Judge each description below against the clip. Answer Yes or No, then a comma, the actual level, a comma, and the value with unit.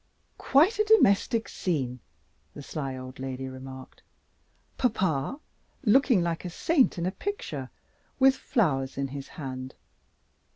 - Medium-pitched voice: Yes, medium, 160 Hz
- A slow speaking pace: Yes, slow, 125 wpm